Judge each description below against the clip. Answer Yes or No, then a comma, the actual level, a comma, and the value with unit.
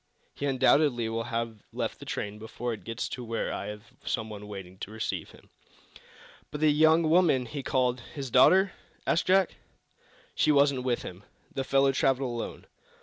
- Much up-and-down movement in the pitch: No, average, 4.3 semitones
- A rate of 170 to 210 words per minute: Yes, average, 175 wpm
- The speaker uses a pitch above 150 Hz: No, low, 125 Hz